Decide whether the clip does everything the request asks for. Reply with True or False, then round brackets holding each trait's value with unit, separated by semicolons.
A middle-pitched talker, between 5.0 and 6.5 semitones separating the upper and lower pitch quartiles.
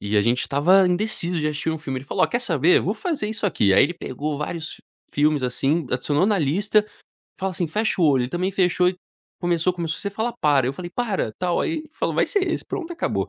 True (175 Hz; 5.6 semitones)